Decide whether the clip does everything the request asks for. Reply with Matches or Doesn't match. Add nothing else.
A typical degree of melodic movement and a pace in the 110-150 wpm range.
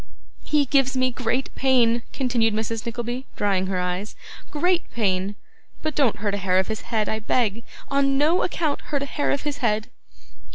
Doesn't match